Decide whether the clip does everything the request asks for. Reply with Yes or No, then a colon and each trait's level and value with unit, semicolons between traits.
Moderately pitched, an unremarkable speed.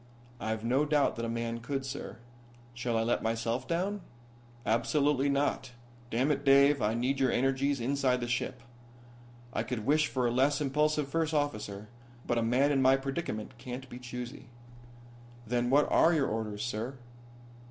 No: low, 130 Hz; average, 165 wpm